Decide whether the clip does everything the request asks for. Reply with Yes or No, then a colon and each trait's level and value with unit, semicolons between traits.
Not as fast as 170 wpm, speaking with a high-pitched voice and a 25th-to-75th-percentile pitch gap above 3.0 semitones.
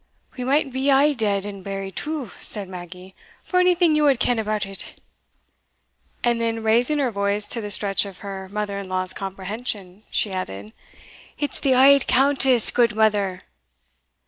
Yes: average, 160 wpm; high, 215 Hz; average, 5.1 semitones